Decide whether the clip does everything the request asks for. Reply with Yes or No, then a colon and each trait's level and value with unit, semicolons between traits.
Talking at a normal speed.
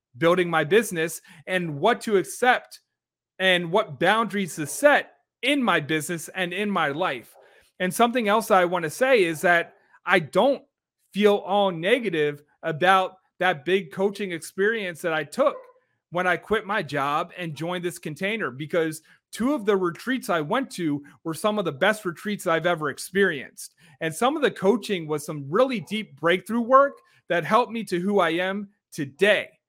Yes: average, 175 wpm